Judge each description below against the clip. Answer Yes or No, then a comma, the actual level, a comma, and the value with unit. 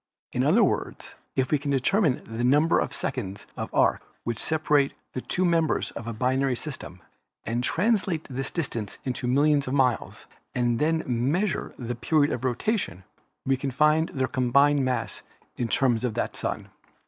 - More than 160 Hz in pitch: No, low, 135 Hz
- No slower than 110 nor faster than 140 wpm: No, average, 175 wpm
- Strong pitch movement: No, average, 3.8 semitones